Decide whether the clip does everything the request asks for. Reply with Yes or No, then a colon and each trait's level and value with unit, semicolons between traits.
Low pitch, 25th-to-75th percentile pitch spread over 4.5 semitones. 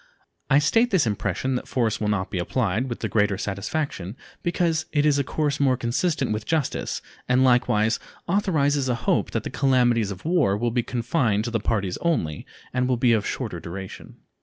Yes: low, 125 Hz; average, 5.3 semitones